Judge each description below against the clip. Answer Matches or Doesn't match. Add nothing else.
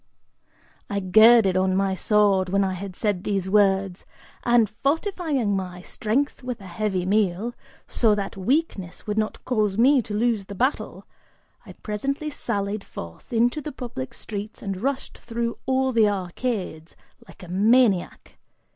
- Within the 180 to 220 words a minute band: Doesn't match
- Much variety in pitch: Doesn't match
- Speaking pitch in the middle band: Doesn't match